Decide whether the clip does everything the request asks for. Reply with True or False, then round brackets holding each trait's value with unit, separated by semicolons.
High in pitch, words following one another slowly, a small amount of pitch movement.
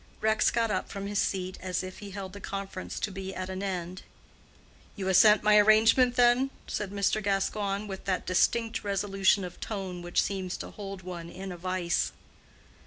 False (195 Hz; 185 wpm; 2.1 semitones)